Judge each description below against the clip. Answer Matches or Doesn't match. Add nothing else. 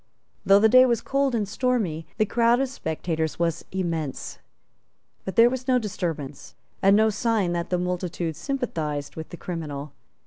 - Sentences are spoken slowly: Doesn't match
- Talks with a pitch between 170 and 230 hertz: Matches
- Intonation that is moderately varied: Doesn't match